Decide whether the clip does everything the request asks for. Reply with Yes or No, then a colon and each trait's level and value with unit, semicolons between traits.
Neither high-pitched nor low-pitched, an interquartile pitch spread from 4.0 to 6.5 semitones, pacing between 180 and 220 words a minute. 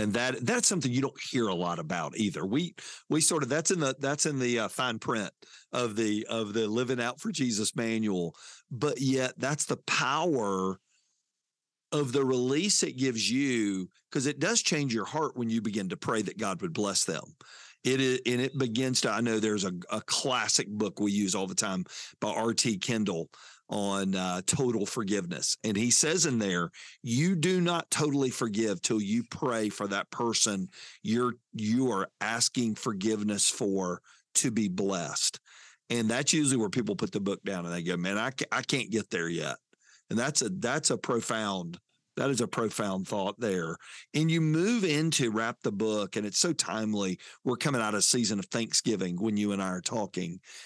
No: low, 115 Hz; average, 4.3 semitones; average, 195 wpm